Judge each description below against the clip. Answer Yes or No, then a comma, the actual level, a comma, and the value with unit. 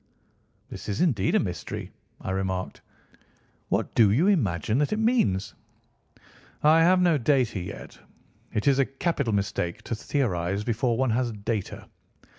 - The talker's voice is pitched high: No, low, 115 Hz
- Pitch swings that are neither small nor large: No, wide, 6.6 semitones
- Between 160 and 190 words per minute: No, average, 145 wpm